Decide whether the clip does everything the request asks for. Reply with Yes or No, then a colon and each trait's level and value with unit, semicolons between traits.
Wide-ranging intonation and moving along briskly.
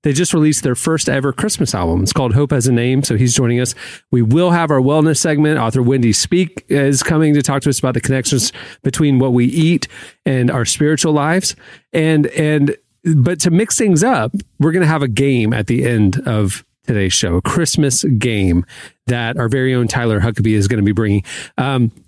No: average, 4.5 semitones; fast, 210 wpm